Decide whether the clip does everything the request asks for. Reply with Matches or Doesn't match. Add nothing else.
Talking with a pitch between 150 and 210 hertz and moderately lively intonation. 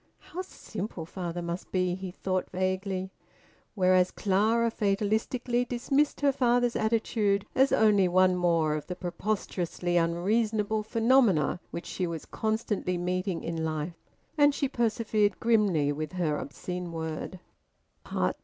Matches